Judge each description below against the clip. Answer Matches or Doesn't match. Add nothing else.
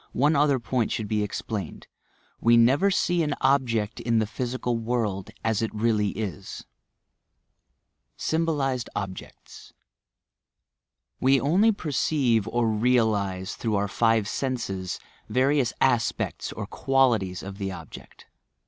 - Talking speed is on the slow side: Matches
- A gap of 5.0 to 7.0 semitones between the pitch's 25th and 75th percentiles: Doesn't match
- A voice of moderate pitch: Doesn't match